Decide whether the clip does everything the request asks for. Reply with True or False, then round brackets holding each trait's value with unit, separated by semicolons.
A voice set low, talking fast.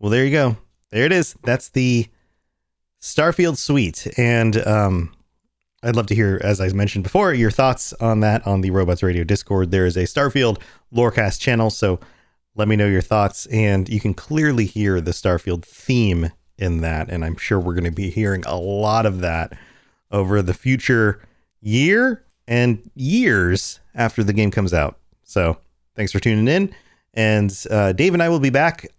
False (105 Hz; 180 wpm)